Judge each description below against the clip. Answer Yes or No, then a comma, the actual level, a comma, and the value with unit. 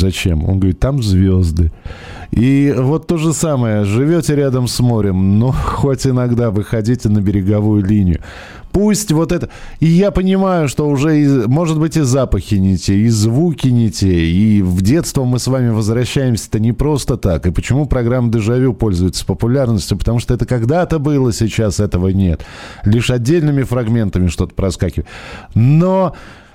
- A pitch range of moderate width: No, wide, 5.7 semitones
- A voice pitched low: Yes, low, 120 Hz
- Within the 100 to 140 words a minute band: No, average, 155 wpm